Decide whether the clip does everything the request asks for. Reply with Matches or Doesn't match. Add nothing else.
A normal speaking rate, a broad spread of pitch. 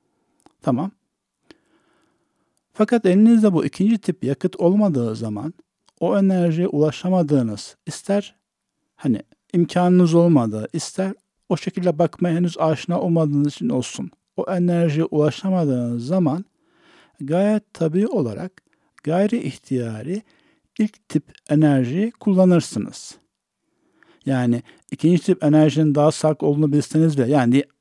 Doesn't match